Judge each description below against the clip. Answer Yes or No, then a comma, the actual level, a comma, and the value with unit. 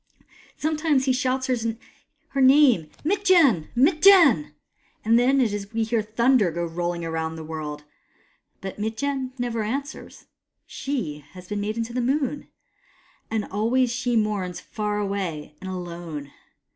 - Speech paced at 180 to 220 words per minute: No, average, 155 wpm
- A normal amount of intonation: No, wide, 6.6 semitones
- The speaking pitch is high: Yes, high, 225 Hz